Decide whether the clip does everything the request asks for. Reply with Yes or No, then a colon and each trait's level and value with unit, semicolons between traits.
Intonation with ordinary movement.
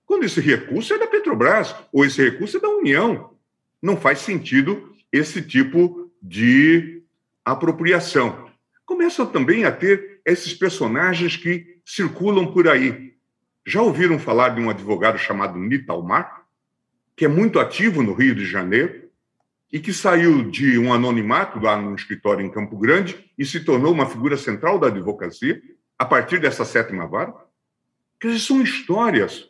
No: wide, 6.7 semitones